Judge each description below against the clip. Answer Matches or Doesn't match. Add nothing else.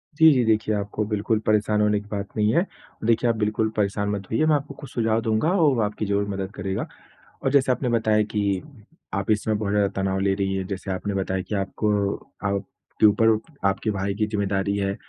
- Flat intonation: Matches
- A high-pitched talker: Doesn't match